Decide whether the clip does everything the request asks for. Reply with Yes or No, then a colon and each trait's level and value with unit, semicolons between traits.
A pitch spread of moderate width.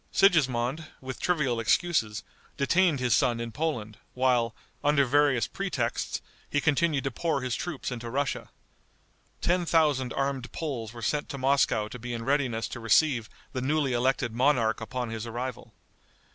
Yes: average, 3.9 semitones